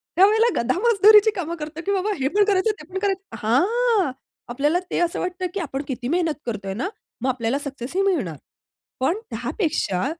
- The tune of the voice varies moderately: No, wide, 7.0 semitones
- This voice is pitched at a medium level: No, very high, 340 Hz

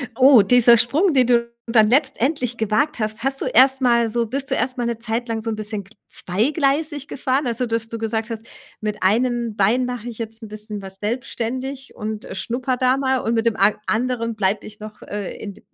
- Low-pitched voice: No, high, 235 Hz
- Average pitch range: Yes, average, 3.0 semitones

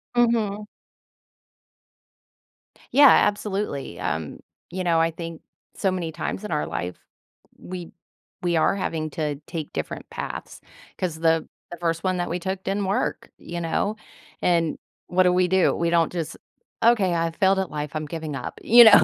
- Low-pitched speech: No, medium, 175 Hz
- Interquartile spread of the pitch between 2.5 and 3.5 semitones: Yes, average, 2.9 semitones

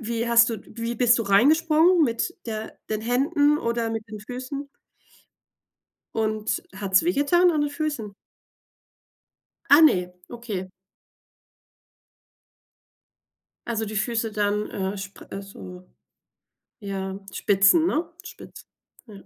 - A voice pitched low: No, high, 230 Hz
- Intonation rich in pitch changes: Yes, wide, 5.7 semitones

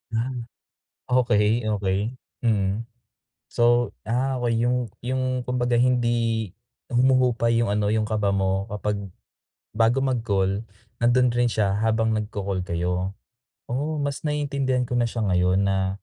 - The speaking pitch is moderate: No, low, 115 Hz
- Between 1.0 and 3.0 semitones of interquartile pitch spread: No, average, 3.5 semitones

